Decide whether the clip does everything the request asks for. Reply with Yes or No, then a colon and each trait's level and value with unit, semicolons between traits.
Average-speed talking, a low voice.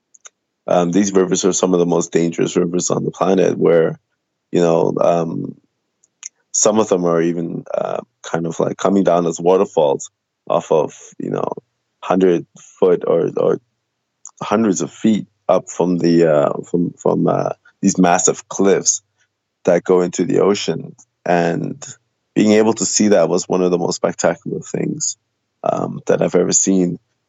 Yes: average, 165 wpm; very low, 90 Hz